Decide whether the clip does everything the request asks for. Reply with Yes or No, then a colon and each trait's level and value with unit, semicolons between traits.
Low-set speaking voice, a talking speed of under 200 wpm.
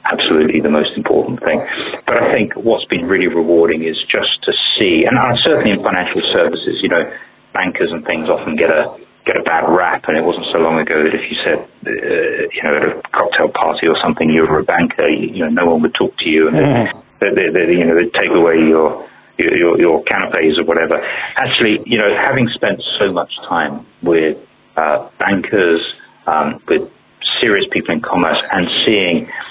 No: very low, 85 Hz; fast, 205 wpm